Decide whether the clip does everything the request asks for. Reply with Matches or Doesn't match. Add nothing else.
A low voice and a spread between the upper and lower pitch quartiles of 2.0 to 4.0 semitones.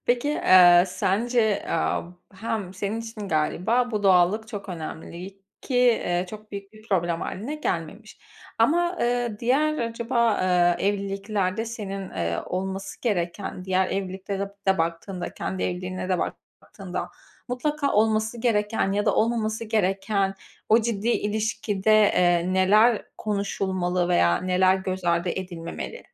Doesn't match